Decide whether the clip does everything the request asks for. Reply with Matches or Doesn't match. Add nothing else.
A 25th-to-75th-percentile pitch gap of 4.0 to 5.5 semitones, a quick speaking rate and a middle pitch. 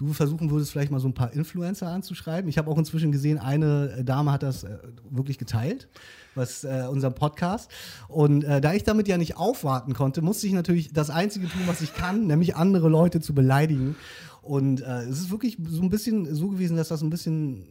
Matches